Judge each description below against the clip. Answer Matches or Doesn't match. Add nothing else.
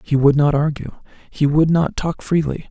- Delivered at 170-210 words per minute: Matches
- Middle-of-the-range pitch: Matches